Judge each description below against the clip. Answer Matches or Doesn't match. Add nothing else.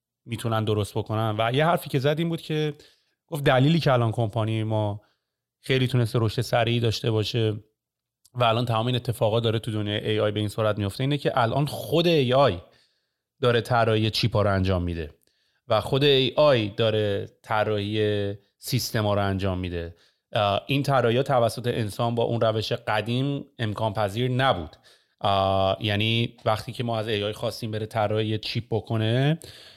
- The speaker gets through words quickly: Matches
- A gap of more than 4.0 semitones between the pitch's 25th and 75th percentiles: Doesn't match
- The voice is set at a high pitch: Doesn't match